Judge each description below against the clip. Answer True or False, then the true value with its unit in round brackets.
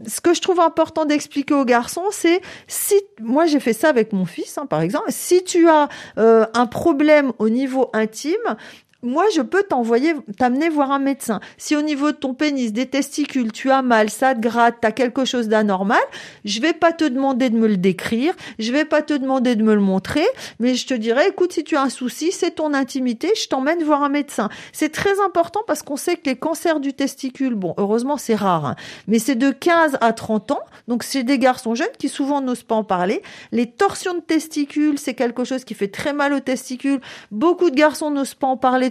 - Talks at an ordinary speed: False (225 wpm)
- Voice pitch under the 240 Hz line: False (275 Hz)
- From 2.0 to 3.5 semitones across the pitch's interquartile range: False (4.7 semitones)